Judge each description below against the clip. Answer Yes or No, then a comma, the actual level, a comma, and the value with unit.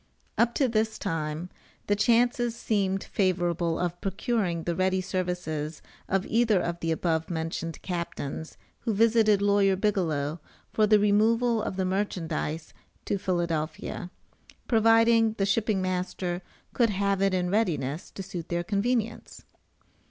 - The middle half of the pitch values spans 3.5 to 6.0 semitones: Yes, average, 4.0 semitones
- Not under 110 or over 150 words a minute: Yes, slow, 135 wpm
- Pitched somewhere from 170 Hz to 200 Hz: Yes, high, 190 Hz